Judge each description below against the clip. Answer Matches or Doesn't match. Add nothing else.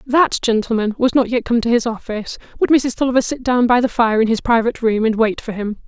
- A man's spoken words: Doesn't match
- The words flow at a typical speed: Doesn't match